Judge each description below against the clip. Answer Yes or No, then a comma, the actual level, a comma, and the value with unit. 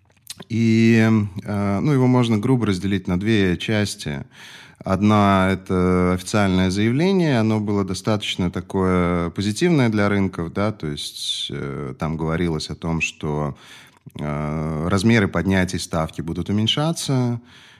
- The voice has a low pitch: Yes, low, 100 Hz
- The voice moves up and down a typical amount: Yes, average, 3.9 semitones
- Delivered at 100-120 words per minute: Yes, slow, 110 wpm